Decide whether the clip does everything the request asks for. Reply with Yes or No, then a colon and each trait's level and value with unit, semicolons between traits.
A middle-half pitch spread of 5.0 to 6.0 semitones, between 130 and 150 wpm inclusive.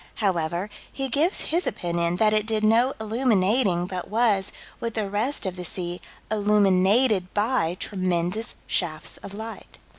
No: average, 3.8 semitones; average, 145 wpm